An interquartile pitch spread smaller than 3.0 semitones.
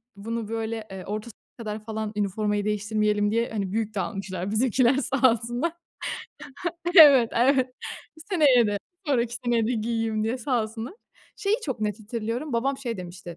Yes: narrow, 2.6 semitones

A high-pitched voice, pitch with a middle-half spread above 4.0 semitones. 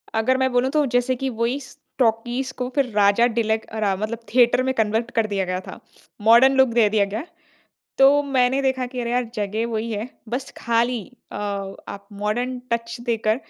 No: high, 235 Hz; average, 2.9 semitones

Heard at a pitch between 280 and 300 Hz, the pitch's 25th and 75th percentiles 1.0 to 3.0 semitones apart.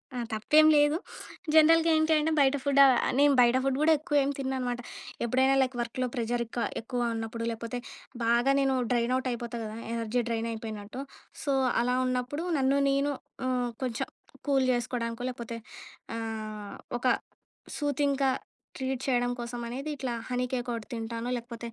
No: very high, 250 Hz; average, 2.7 semitones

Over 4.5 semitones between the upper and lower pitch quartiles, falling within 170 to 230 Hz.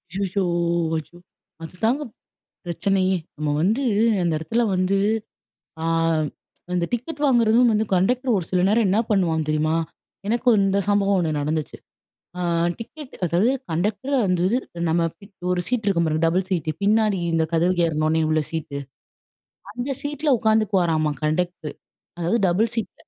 Yes: average, 5.0 semitones; high, 190 Hz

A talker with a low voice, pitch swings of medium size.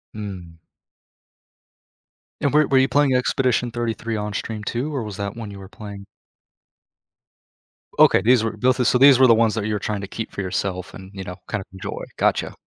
Yes: low, 110 Hz; average, 3.8 semitones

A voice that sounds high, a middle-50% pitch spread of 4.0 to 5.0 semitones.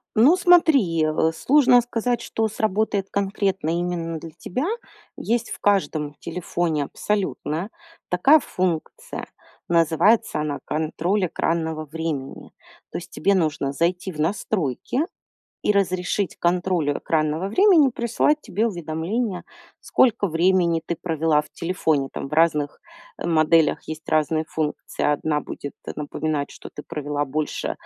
No: medium, 170 Hz; average, 4.7 semitones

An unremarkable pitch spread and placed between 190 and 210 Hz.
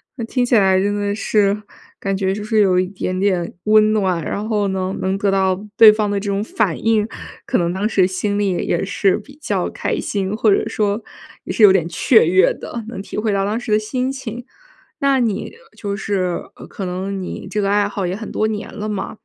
No: narrow, 2.1 semitones; high, 205 Hz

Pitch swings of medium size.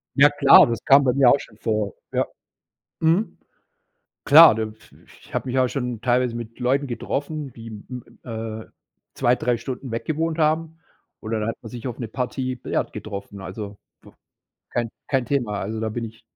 Yes: average, 3.8 semitones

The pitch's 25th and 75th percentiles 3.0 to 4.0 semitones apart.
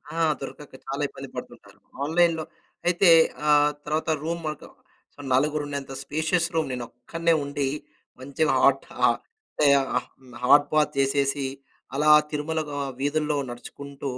No: narrow, 2.6 semitones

